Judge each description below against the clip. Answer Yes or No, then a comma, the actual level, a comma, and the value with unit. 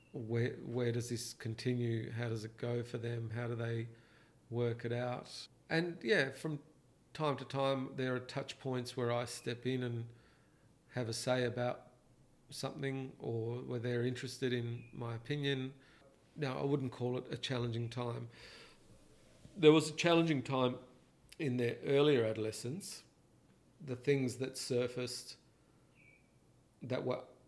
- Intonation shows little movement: Yes, narrow, 2.1 semitones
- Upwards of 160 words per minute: No, average, 145 wpm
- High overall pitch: No, low, 125 Hz